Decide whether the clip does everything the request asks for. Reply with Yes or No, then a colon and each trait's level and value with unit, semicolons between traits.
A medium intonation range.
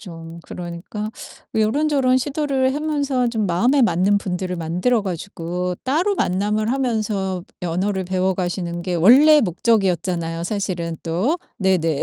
No: wide, 6.0 semitones